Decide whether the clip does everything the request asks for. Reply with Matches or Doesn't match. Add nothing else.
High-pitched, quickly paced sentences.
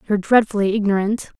Doesn't match